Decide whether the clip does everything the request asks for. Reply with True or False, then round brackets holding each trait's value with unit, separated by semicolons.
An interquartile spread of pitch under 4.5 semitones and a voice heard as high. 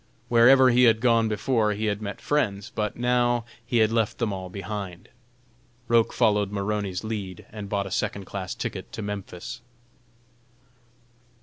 False (2.8 semitones; 105 Hz)